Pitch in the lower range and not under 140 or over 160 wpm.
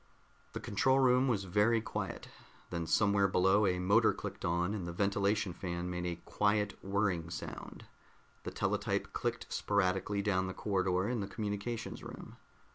Yes: low, 100 Hz; average, 155 wpm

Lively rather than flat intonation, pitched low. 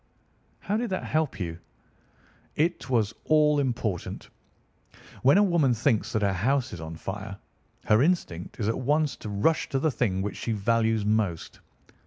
Yes: wide, 6.7 semitones; low, 115 Hz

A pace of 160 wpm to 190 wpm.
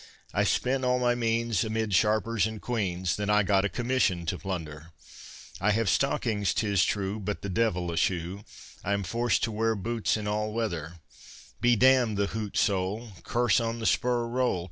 Yes: average, 185 wpm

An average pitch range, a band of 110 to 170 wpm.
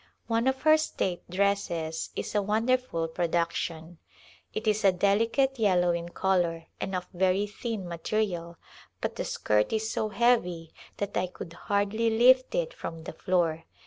Yes: average, 4.6 semitones; average, 160 wpm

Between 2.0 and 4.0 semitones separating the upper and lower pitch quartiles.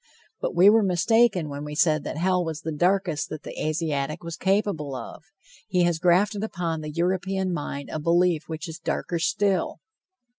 Yes: average, 3.3 semitones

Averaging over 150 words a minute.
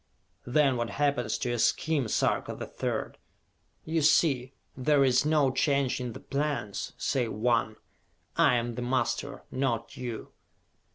No: average, 140 wpm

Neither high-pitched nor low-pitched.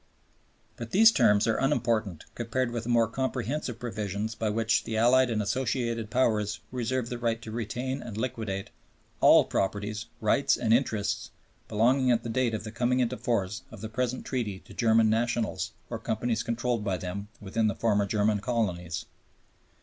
No: low, 115 Hz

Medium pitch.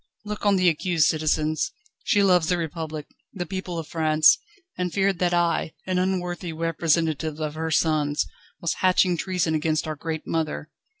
Yes: medium, 165 Hz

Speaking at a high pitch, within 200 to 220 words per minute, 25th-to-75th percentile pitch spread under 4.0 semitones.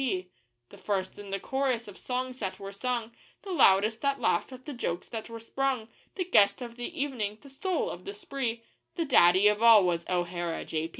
No: high, 230 Hz; fast, 205 wpm; average, 5.3 semitones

